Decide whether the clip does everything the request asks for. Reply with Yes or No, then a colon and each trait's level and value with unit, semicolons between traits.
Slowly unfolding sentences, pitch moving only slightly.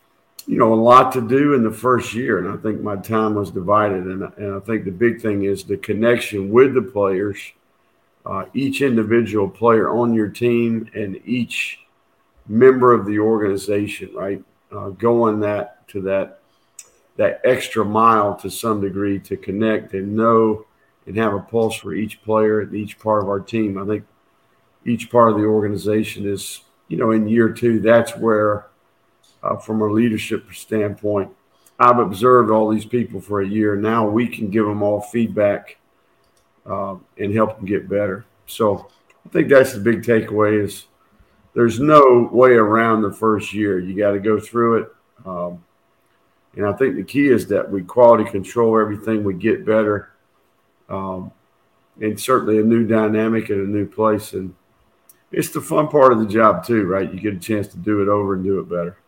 No: average, 185 wpm; narrow, 2.2 semitones